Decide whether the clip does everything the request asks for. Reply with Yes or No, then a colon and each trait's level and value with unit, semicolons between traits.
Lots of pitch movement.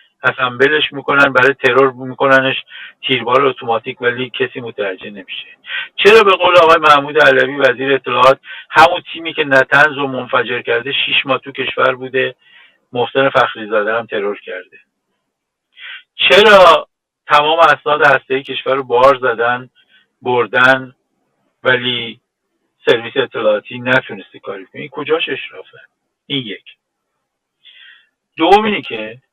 No: average, 3.8 semitones